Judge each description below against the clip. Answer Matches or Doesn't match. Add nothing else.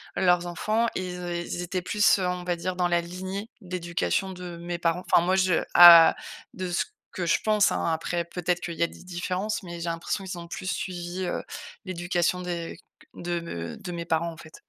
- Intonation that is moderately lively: Doesn't match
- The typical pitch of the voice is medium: Matches